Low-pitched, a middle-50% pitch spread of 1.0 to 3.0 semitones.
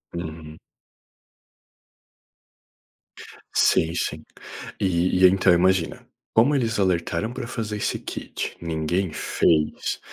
No: very low, 90 Hz; average, 4.0 semitones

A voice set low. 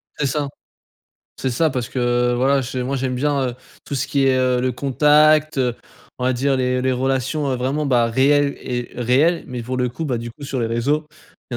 Yes: low, 130 Hz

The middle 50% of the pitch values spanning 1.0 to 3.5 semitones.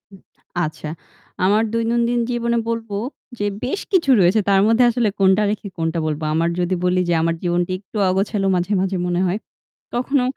No: average, 4.6 semitones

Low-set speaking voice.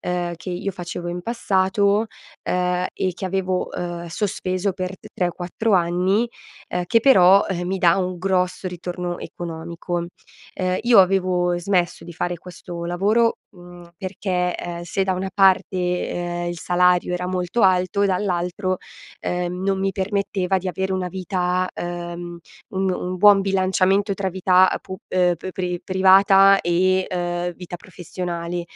No: medium, 180 Hz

